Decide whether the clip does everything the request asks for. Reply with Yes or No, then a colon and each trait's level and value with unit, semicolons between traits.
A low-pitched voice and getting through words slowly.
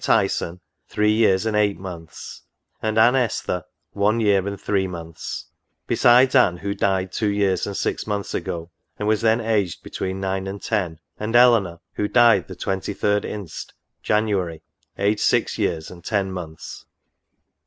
No: low, 100 Hz; average, 155 wpm